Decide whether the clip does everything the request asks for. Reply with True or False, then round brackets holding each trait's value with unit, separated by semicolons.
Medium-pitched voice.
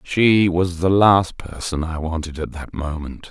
False (85 Hz)